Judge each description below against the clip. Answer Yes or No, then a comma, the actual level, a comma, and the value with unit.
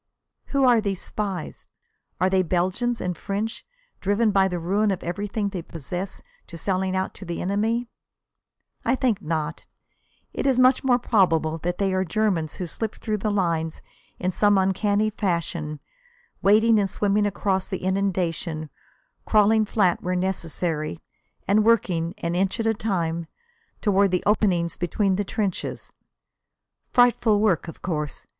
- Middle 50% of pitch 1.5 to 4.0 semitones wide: Yes, average, 3.4 semitones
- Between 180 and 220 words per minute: No, average, 150 wpm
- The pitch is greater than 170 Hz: Yes, high, 190 Hz